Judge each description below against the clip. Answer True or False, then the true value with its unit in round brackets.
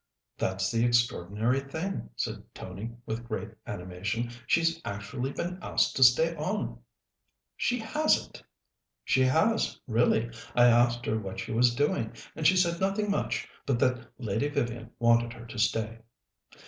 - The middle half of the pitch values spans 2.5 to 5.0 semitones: False (5.5 semitones)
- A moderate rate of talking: True (150 wpm)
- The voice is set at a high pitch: False (120 Hz)